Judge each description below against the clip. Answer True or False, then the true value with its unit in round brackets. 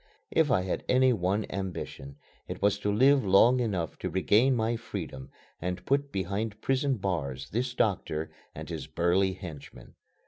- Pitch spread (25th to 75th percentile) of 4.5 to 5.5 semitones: True (5.1 semitones)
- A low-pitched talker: True (100 Hz)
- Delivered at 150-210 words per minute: True (160 wpm)